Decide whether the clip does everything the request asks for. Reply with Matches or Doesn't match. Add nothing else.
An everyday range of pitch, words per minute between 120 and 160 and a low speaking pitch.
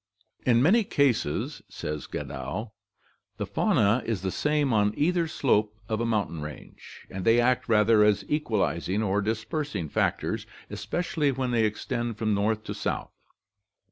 Matches